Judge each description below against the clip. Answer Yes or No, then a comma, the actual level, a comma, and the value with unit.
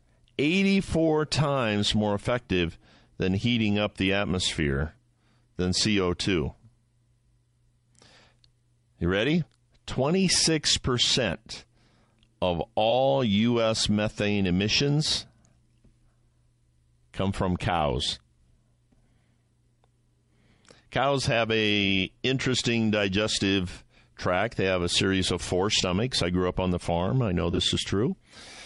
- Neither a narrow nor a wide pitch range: Yes, average, 4.2 semitones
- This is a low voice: Yes, low, 110 Hz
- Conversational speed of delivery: No, slow, 95 wpm